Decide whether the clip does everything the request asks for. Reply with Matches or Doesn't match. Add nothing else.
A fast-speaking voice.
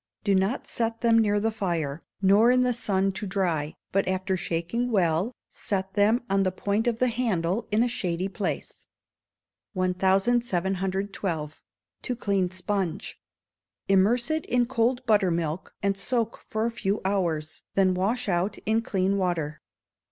Doesn't match